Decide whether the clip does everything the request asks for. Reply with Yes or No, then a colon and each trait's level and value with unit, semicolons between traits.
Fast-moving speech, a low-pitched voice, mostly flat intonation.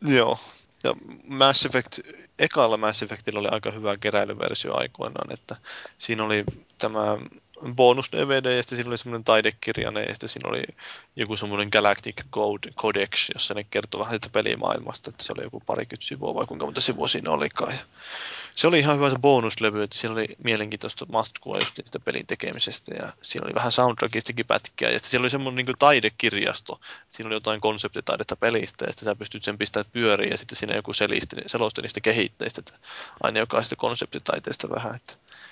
No: fast, 175 wpm; low, 115 Hz; average, 3.2 semitones